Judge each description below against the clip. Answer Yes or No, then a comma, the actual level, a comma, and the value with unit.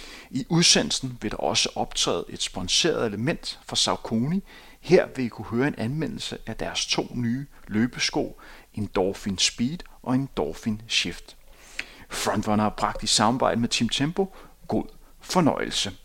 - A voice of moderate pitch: No, low, 120 Hz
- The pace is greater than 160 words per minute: No, slow, 145 wpm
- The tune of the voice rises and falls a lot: No, average, 4.3 semitones